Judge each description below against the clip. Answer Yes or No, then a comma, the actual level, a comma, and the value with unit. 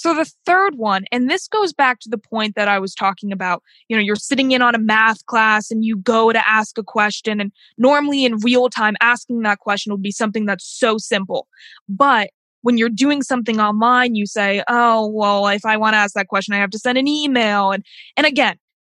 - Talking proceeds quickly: Yes, fast, 230 wpm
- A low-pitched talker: No, high, 220 Hz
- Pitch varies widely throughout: No, average, 3.4 semitones